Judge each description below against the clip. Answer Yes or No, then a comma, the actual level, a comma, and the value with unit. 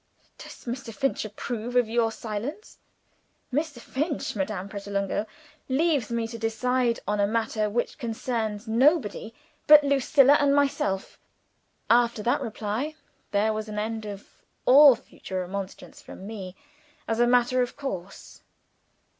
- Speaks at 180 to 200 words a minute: No, slow, 135 wpm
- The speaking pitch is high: Yes, high, 230 Hz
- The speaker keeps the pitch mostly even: No, average, 3.6 semitones